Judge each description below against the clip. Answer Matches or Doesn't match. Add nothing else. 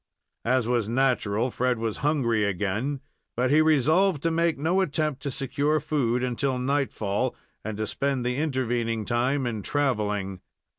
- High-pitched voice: Doesn't match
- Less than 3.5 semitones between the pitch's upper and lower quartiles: Doesn't match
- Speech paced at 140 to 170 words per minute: Matches